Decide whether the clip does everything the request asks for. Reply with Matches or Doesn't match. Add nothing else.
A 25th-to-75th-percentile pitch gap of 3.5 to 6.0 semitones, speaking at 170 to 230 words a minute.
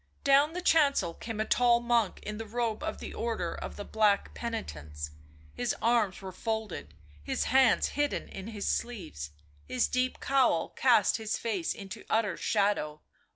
Doesn't match